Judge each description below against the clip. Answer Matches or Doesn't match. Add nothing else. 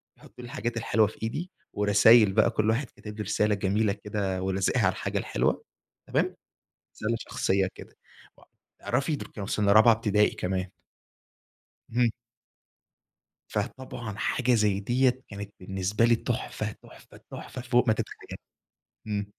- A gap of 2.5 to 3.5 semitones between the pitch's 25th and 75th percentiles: Matches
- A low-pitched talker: Matches